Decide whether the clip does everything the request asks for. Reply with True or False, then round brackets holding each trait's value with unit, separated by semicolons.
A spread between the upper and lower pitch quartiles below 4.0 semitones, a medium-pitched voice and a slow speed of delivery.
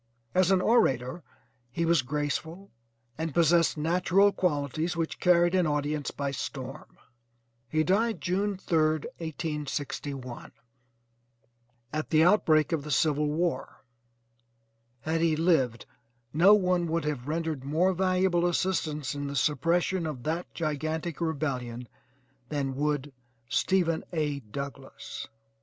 True (3.3 semitones; 160 Hz; 120 wpm)